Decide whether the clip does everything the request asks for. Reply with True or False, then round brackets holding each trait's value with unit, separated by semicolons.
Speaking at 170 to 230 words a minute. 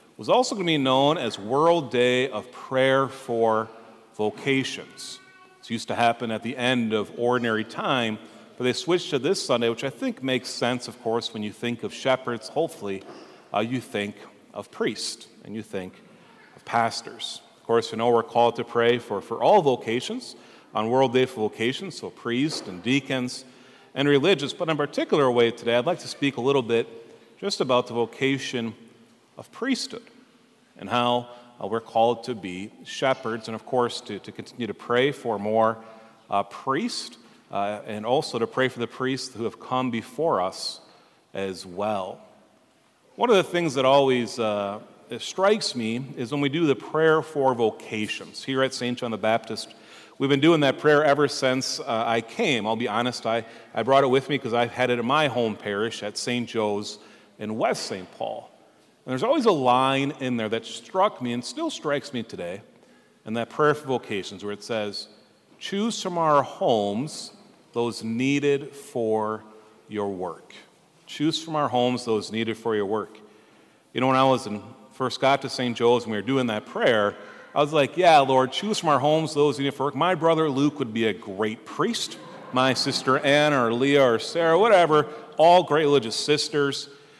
True (190 wpm)